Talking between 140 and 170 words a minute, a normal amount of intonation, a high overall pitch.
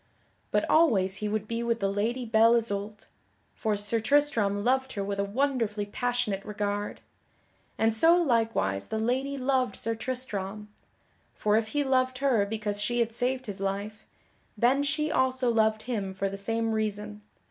Yes: average, 165 wpm; average, 3.6 semitones; high, 220 Hz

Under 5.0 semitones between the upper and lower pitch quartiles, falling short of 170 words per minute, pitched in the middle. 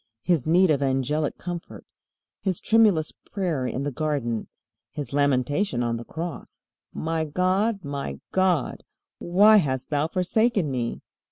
No: average, 5.3 semitones; slow, 135 wpm; medium, 155 Hz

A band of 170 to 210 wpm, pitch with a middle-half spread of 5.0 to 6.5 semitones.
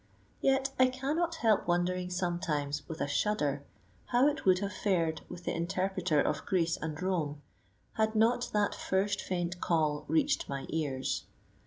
No: average, 155 wpm; average, 5.3 semitones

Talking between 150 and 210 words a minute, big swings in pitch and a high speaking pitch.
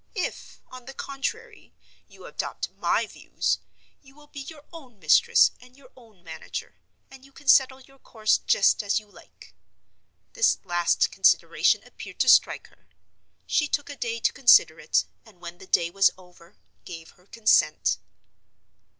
Yes: average, 160 wpm; wide, 7.1 semitones; high, 240 Hz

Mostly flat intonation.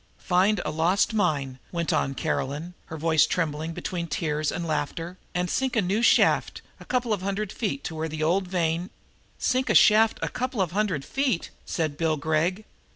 No: average, 4.6 semitones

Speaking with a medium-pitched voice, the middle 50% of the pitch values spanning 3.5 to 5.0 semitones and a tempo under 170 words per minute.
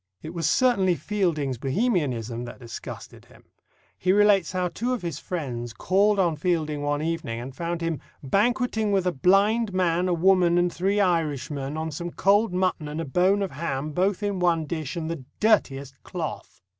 No: medium, 170 Hz; average, 4.7 semitones; average, 180 wpm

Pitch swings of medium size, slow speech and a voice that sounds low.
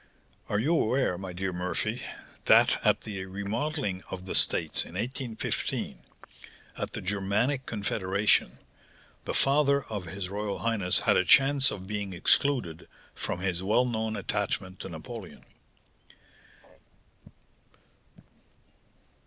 Yes: average, 4.7 semitones; slow, 120 wpm; low, 105 Hz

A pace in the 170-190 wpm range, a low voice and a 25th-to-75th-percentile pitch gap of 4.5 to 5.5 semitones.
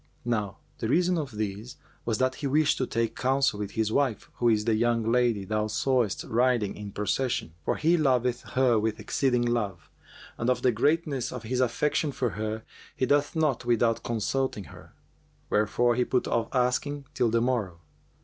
No: average, 180 wpm; low, 120 Hz; average, 3.2 semitones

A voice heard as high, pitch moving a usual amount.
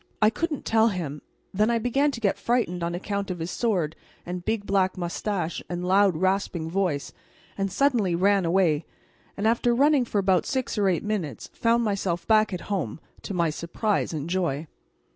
Yes: high, 195 Hz; average, 4.1 semitones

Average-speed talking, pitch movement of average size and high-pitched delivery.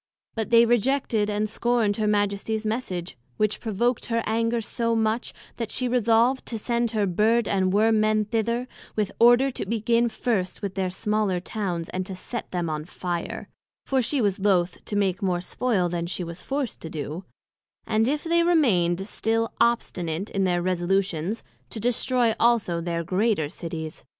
Yes: average, 170 wpm; average, 4.2 semitones; high, 215 Hz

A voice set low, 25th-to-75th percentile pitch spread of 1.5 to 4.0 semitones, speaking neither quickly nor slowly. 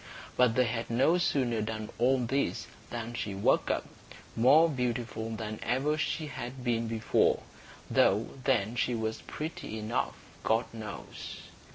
Yes: low, 120 Hz; narrow, 2.6 semitones; average, 145 wpm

